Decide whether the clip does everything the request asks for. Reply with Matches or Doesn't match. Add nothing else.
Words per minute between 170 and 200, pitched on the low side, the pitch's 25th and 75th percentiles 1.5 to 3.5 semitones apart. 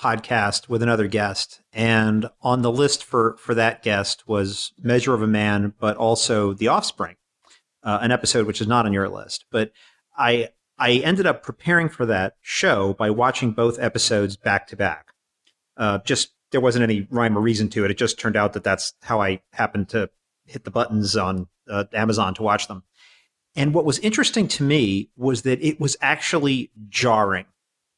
Matches